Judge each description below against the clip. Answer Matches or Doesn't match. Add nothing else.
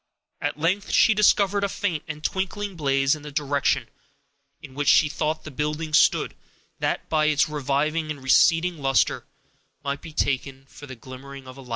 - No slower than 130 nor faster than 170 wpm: Doesn't match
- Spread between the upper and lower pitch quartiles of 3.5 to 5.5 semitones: Doesn't match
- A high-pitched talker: Doesn't match